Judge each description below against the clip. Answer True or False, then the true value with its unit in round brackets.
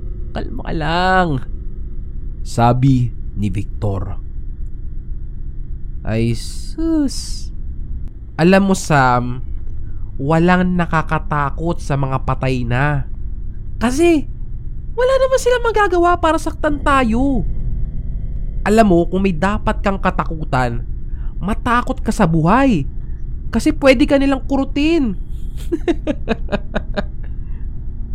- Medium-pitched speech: True (160 Hz)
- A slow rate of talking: True (85 wpm)